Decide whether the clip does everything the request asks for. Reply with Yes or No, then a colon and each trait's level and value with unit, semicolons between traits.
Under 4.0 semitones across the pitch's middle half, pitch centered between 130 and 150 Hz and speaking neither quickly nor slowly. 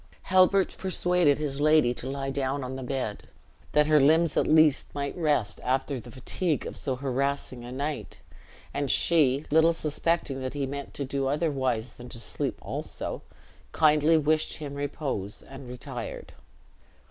Yes: average, 2.8 semitones; medium, 140 Hz; average, 160 wpm